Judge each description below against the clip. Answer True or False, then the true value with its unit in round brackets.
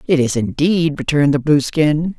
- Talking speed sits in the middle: True (165 wpm)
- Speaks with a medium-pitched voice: True (150 Hz)